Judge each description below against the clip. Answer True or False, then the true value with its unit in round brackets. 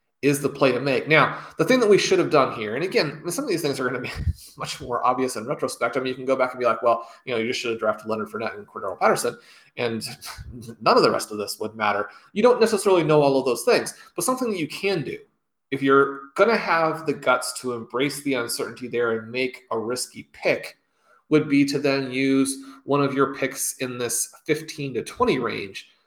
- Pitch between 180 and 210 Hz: False (135 Hz)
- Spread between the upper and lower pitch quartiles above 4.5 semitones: False (3.4 semitones)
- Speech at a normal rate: False (245 wpm)